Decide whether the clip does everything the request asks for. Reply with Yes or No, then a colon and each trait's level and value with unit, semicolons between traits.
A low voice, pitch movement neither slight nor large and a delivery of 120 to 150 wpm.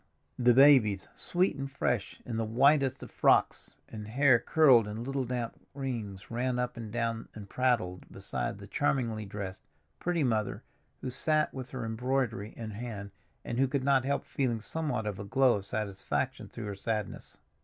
No: low, 120 Hz; average, 3.8 semitones; average, 175 wpm